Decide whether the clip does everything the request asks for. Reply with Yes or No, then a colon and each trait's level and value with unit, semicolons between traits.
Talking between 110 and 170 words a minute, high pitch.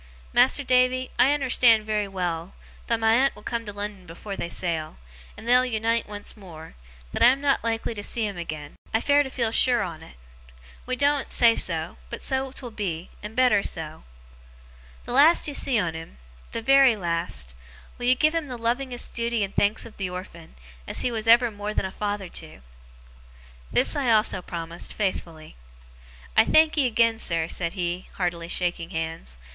No: average, 185 wpm; high, 220 Hz